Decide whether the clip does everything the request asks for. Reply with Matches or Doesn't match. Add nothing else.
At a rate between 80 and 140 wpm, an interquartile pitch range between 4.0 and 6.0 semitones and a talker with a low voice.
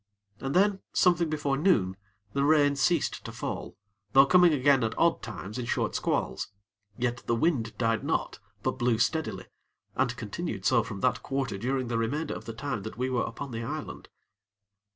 Doesn't match